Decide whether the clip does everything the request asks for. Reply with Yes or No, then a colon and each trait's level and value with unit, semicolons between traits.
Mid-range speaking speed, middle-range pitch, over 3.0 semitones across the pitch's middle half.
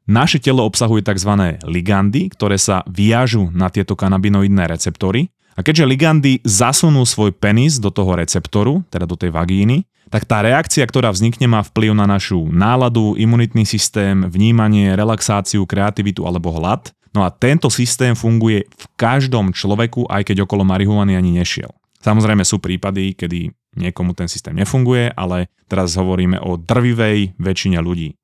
No: average, 150 wpm; low, 105 Hz; average, 3.9 semitones